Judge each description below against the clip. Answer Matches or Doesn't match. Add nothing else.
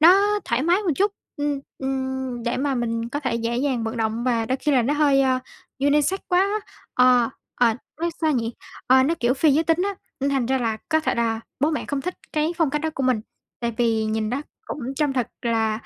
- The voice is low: Doesn't match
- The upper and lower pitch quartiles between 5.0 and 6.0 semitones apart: Doesn't match